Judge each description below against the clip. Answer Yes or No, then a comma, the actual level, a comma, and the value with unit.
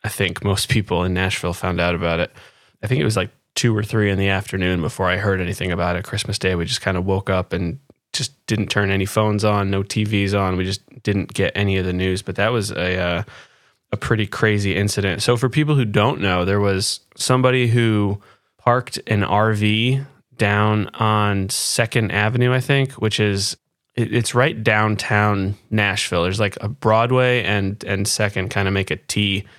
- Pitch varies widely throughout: No, narrow, 2.6 semitones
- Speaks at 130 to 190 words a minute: No, average, 200 wpm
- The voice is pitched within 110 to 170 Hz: No, low, 100 Hz